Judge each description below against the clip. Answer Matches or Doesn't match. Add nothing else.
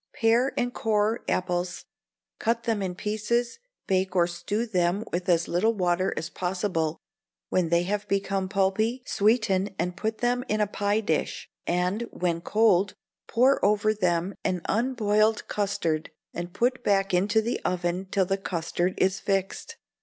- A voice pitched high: Matches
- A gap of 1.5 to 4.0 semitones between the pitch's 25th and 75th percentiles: Matches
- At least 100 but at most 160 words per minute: Matches